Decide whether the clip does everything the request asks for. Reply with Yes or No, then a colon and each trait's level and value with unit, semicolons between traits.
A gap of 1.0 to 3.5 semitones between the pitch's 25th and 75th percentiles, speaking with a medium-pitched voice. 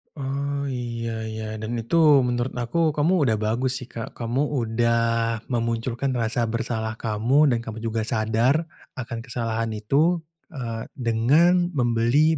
No: average, 3.2 semitones; low, 120 Hz